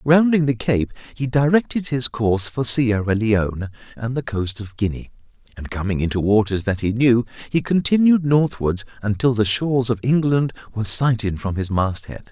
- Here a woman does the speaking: No, male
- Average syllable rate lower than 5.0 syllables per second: No, 5.1 syllables/s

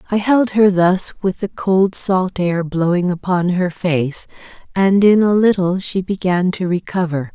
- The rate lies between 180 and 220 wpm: No, average, 170 wpm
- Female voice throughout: Yes, female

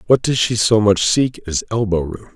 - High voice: No, low, 110 Hz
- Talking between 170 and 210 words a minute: Yes, fast, 205 wpm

